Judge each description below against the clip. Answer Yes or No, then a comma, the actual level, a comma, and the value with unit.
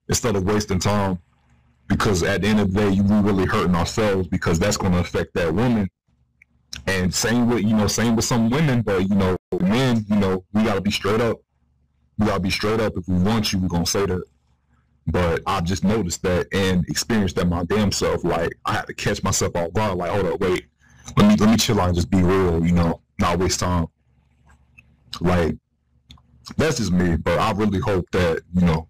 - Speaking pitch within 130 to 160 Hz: No, very low, 95 Hz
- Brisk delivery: Yes, fast, 215 wpm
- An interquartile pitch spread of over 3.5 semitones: Yes, average, 4.2 semitones